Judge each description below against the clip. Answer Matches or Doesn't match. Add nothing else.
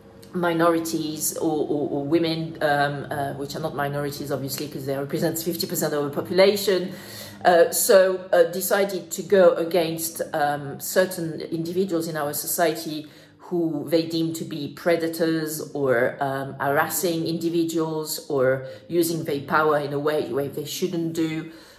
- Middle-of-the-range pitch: Matches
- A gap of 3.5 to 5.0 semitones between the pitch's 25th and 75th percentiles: Doesn't match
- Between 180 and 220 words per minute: Doesn't match